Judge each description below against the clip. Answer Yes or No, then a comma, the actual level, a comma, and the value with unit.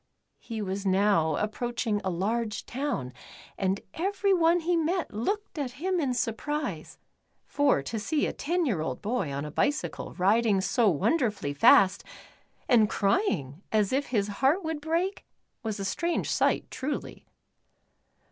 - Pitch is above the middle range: Yes, high, 230 Hz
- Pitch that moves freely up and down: Yes, wide, 7.6 semitones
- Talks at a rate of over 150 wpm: No, average, 145 wpm